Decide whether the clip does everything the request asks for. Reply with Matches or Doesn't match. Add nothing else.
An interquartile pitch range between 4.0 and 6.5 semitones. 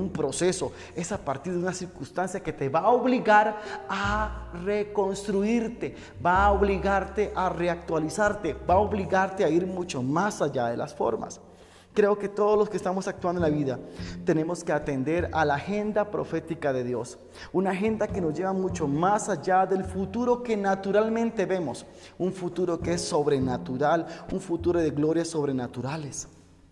Matches